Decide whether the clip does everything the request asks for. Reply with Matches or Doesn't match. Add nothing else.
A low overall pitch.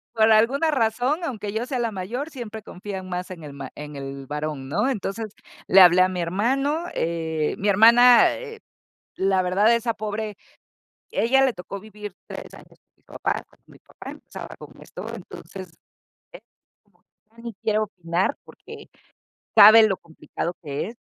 Doesn't match